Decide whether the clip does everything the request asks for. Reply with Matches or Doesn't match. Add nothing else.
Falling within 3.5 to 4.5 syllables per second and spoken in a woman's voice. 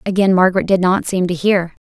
Doesn't match